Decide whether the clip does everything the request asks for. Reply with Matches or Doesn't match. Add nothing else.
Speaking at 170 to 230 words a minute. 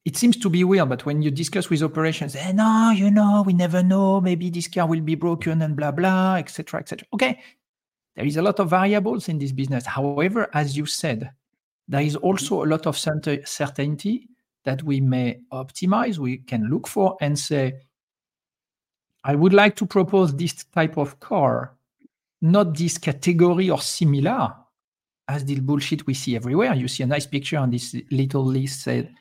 Matches